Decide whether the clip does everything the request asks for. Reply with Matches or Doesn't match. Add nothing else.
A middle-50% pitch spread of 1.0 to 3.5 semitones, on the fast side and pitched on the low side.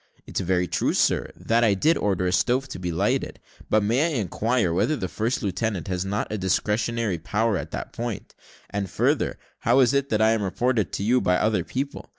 Doesn't match